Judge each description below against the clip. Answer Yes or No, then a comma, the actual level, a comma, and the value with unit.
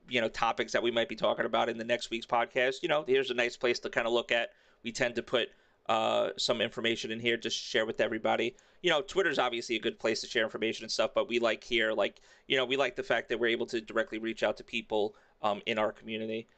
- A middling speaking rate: No, fast, 270 wpm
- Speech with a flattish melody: Yes, narrow, 1.0 semitones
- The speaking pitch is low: Yes, low, 115 Hz